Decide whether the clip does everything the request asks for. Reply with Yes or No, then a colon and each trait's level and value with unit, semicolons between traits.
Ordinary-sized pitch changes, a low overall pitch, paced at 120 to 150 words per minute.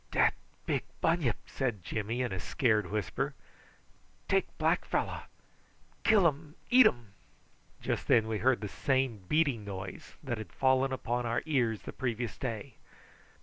Yes: average, 3.8 semitones; low, 120 Hz; average, 145 wpm